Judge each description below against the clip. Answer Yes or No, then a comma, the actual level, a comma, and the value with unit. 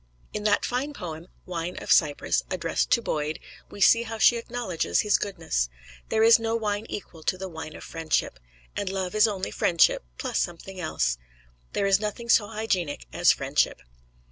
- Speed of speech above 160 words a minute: Yes, average, 175 wpm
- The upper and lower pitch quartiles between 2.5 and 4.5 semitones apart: No, average, 5.1 semitones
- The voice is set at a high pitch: Yes, high, 195 Hz